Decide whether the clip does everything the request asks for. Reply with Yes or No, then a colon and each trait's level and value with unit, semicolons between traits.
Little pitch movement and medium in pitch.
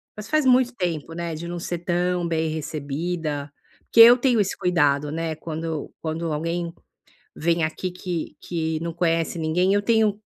Yes: narrow, 2.3 semitones; medium, 170 Hz